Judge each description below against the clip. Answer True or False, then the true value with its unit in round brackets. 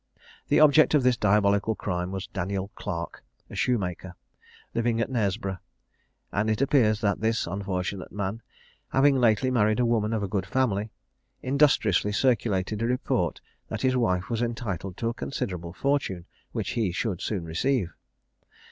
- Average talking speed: True (155 wpm)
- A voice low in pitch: True (105 Hz)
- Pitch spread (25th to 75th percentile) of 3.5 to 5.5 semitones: True (4.1 semitones)